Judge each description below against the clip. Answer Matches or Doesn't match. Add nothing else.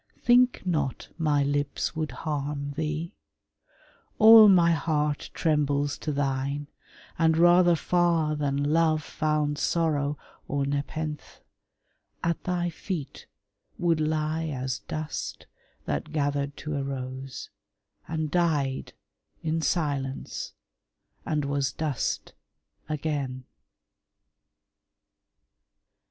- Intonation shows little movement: Matches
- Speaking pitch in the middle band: Matches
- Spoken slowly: Matches